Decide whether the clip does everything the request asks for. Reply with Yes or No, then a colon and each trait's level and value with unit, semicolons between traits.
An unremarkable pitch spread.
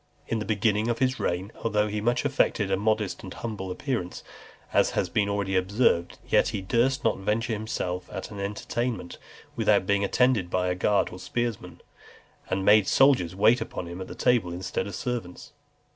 Yes: average, 3.7 semitones